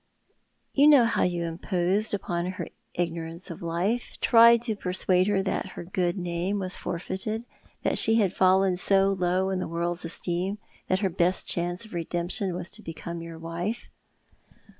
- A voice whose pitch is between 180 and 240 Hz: Yes, medium, 185 Hz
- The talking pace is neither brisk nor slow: Yes, average, 165 wpm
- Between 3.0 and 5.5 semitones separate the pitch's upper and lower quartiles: No, narrow, 2.5 semitones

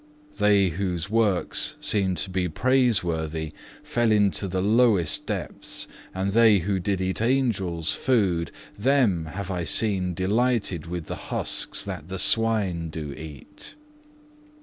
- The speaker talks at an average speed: No, slow, 130 wpm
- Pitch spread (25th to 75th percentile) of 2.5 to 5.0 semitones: Yes, average, 4.1 semitones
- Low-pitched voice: Yes, very low, 95 Hz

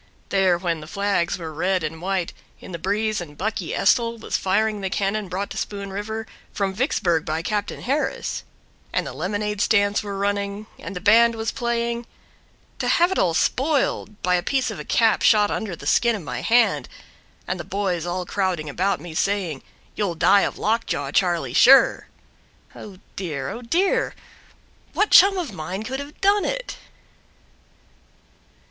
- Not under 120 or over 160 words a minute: No, average, 175 wpm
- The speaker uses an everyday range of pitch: Yes, average, 4.0 semitones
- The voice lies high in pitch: Yes, high, 200 Hz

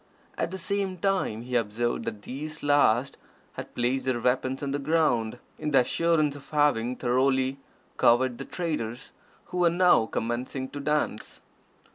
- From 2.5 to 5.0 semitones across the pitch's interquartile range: Yes, average, 4.2 semitones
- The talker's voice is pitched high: No, low, 135 Hz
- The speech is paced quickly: No, average, 155 wpm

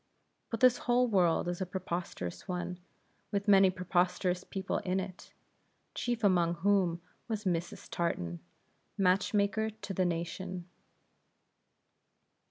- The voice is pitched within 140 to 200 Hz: Yes, medium, 185 Hz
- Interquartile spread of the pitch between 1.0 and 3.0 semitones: Yes, narrow, 2.5 semitones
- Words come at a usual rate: No, slow, 120 wpm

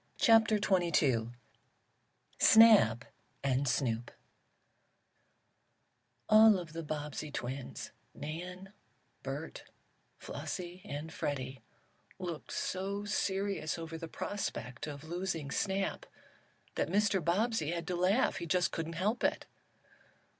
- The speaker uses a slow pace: Yes, slow, 105 wpm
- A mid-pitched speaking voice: Yes, medium, 170 Hz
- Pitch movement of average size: Yes, average, 4.8 semitones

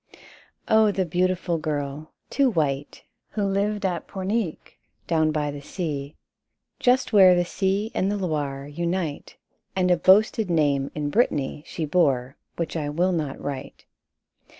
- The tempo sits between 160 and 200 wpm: No, average, 145 wpm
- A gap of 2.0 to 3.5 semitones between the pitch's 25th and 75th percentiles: No, average, 4.7 semitones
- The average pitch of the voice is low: No, medium, 170 Hz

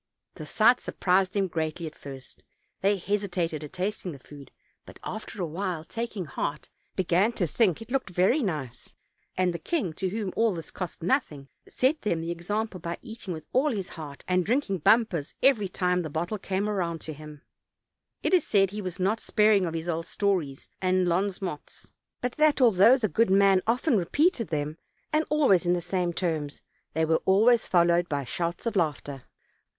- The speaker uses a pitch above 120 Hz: Yes, medium, 185 Hz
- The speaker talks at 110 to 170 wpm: No, average, 190 wpm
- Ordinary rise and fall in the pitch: Yes, average, 4.6 semitones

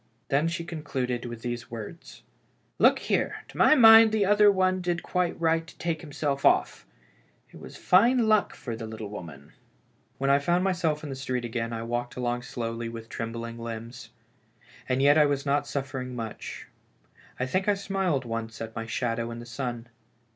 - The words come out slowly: No, average, 185 wpm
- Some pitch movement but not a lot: No, wide, 6.5 semitones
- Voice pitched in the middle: No, low, 130 Hz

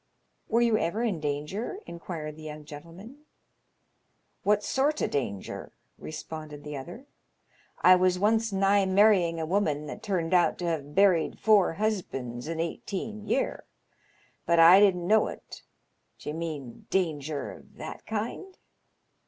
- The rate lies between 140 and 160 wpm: Yes, average, 145 wpm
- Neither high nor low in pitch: Yes, medium, 180 Hz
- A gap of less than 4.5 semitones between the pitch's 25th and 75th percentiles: No, average, 5.2 semitones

